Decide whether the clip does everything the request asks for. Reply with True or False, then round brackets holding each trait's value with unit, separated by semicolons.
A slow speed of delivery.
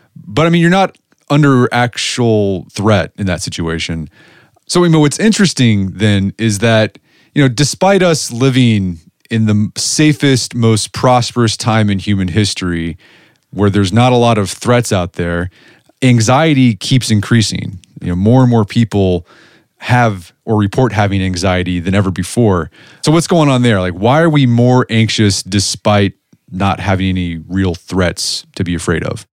False (165 wpm)